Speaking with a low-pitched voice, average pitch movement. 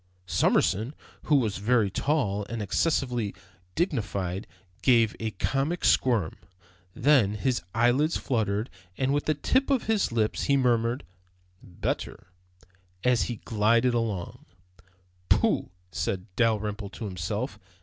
Yes: low, 115 Hz; average, 4.4 semitones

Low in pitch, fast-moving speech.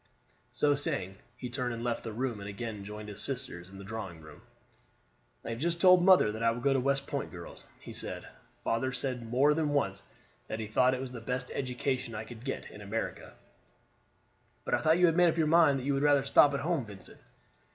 Yes: low, 125 Hz; fast, 225 wpm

